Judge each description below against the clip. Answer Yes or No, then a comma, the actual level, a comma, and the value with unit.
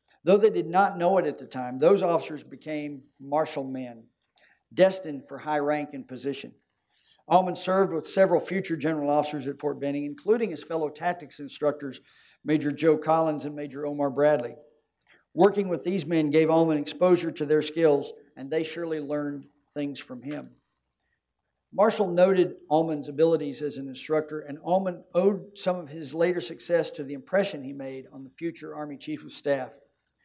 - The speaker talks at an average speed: Yes, average, 170 wpm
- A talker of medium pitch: Yes, medium, 150 Hz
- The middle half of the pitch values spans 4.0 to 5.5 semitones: No, average, 3.1 semitones